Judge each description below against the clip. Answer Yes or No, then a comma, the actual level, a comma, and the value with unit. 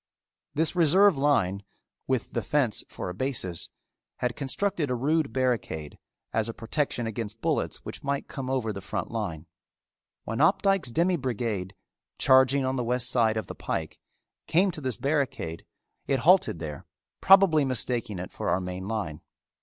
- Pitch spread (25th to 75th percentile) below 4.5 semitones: No, wide, 5.6 semitones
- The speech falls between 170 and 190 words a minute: No, average, 160 wpm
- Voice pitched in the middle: No, low, 125 Hz